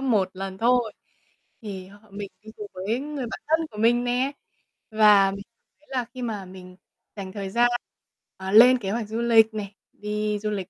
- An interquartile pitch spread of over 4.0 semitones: No, average, 3.4 semitones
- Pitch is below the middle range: No, high, 215 Hz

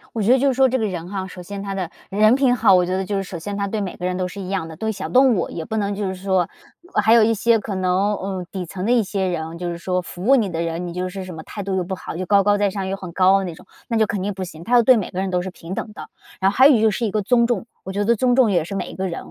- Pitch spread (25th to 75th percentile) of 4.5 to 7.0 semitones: No, average, 3.0 semitones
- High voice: Yes, high, 195 Hz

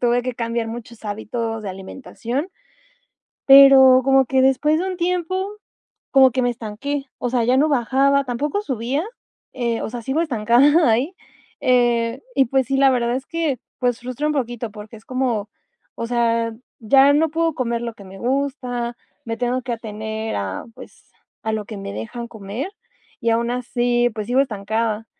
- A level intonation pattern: No, average, 3.0 semitones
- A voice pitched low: No, high, 245 Hz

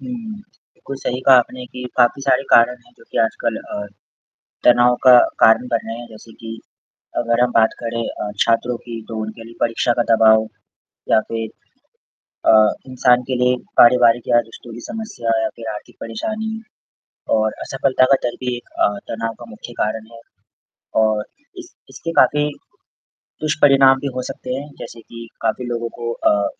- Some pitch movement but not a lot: No, narrow, 2.2 semitones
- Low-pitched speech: Yes, low, 120 Hz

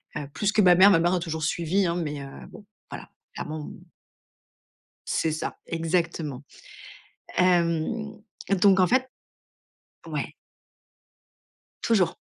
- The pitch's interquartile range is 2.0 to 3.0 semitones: No, average, 3.6 semitones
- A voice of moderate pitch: Yes, medium, 175 Hz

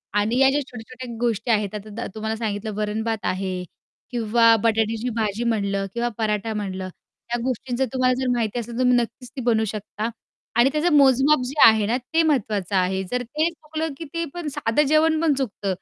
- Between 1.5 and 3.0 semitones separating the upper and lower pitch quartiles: No, average, 3.6 semitones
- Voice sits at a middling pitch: No, high, 235 Hz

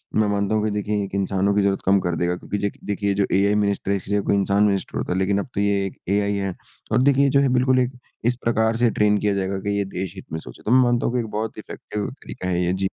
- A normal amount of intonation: No, narrow, 1.9 semitones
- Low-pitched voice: Yes, low, 100 Hz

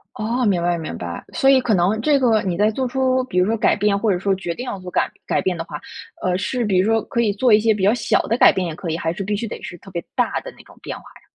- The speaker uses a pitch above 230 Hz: No, high, 205 Hz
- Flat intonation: No, average, 4.2 semitones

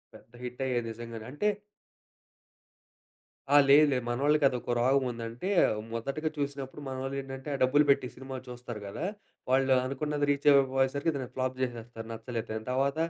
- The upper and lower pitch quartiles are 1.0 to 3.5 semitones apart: Yes, narrow, 2.5 semitones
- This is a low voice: Yes, low, 130 Hz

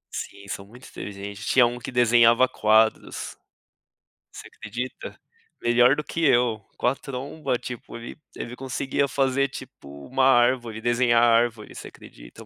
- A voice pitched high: No, low, 120 Hz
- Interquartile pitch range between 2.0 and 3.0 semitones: Yes, narrow, 2.5 semitones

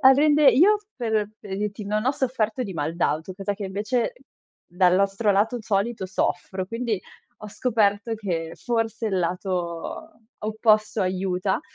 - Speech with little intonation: No, average, 3.5 semitones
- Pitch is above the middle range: Yes, high, 210 Hz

